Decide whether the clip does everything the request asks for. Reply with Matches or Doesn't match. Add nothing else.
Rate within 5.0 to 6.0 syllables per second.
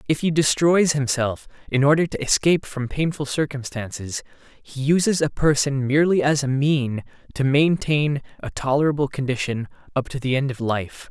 Matches